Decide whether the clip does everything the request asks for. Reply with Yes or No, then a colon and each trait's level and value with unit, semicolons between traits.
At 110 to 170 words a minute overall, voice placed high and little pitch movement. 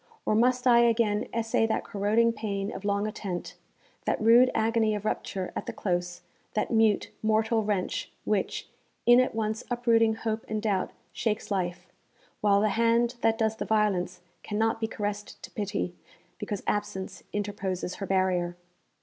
Yes: average, 160 wpm; high, 215 Hz; narrow, 2.2 semitones